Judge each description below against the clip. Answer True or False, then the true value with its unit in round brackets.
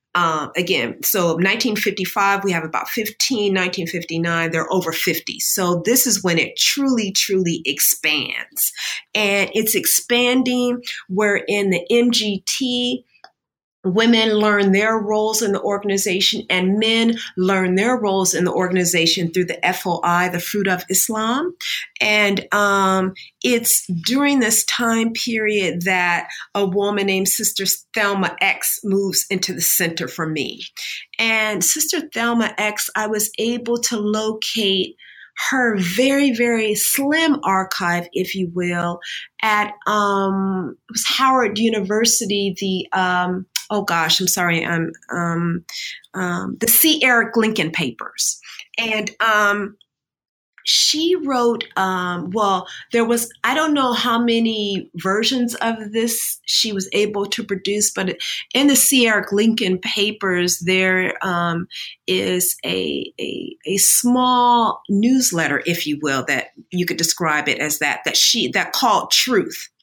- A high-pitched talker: True (205 Hz)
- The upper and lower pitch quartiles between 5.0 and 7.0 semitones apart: False (3.9 semitones)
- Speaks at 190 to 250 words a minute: False (135 wpm)